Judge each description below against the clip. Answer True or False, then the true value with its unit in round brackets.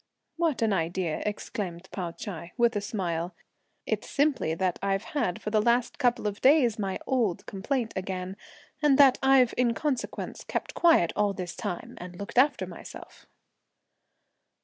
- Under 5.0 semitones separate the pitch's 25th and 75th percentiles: False (5.5 semitones)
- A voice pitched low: False (210 Hz)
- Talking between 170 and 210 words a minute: False (155 wpm)